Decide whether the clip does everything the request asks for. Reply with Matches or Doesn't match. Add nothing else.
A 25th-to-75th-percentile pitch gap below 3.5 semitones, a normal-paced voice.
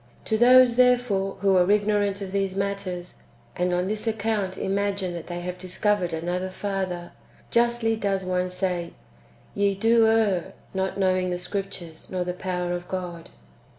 Matches